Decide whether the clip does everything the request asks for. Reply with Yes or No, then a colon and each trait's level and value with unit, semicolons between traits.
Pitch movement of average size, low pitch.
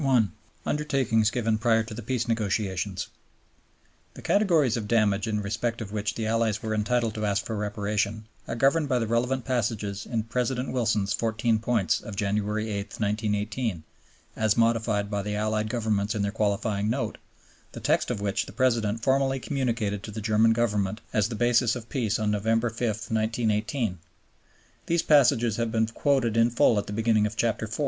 No: narrow, 2.1 semitones; low, 110 Hz